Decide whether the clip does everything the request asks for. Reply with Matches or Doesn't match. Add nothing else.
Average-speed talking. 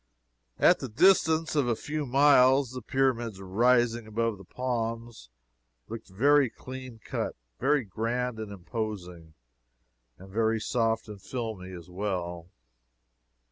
Doesn't match